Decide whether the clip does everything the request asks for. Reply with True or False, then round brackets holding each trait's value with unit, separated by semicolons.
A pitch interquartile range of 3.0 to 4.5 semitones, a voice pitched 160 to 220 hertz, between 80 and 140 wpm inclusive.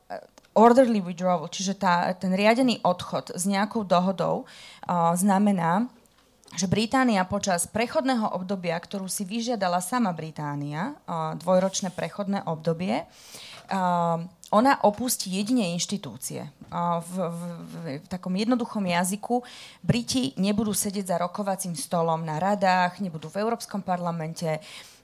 True (3.4 semitones; 190 Hz; 125 wpm)